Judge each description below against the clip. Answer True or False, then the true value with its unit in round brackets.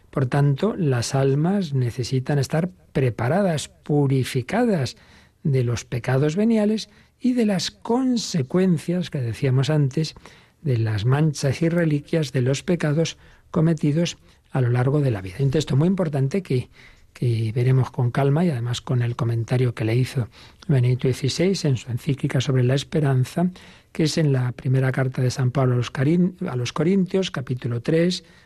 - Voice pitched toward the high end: False (140 Hz)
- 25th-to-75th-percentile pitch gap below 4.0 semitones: False (4.7 semitones)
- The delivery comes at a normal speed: True (160 wpm)